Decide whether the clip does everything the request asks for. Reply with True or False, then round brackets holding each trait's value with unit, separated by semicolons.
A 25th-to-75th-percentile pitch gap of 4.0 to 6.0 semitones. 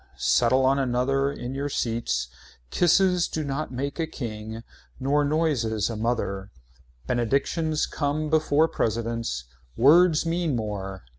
True (5.0 semitones)